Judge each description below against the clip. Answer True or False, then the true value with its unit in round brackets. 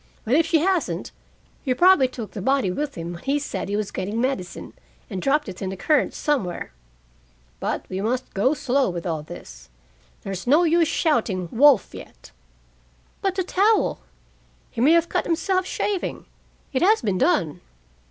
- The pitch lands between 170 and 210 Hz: False (260 Hz)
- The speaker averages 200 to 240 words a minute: False (170 wpm)